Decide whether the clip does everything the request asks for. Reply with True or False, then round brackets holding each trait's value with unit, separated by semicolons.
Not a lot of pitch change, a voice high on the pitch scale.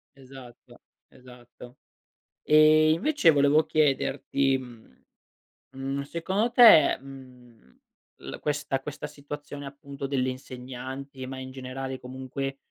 False (2.0 semitones; 135 Hz)